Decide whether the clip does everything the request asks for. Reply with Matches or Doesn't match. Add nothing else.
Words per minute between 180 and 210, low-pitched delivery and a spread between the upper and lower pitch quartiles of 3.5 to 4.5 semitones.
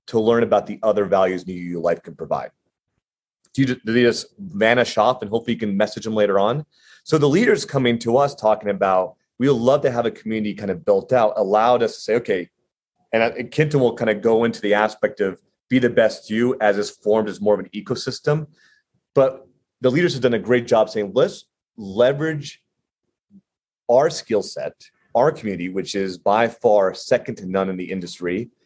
Matches